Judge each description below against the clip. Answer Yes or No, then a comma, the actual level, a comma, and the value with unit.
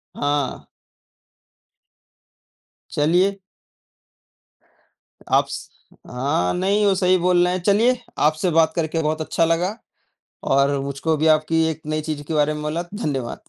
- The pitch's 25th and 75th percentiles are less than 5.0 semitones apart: Yes, average, 3.2 semitones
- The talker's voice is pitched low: No, medium, 160 Hz